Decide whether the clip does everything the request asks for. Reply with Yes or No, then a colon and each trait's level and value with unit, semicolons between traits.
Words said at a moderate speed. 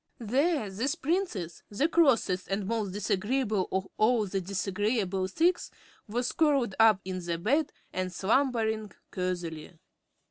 No: slow, 120 wpm